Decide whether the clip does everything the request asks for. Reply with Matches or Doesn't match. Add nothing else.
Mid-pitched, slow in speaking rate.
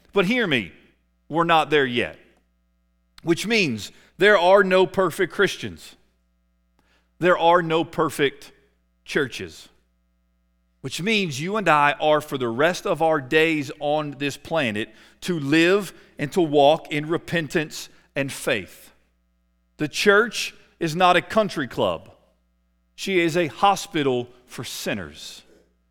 Matches